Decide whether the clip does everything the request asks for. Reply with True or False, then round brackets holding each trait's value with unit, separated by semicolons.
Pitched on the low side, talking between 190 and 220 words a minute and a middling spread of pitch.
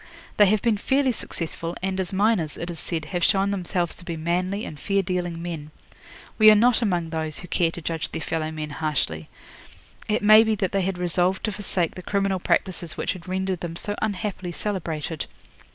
False (180 Hz; 200 wpm; 3.3 semitones)